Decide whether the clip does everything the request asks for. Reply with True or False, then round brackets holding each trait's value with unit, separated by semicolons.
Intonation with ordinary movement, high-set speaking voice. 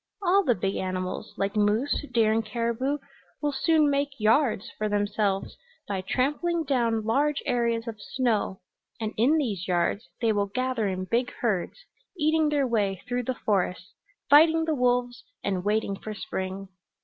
True (5.0 semitones; 230 Hz)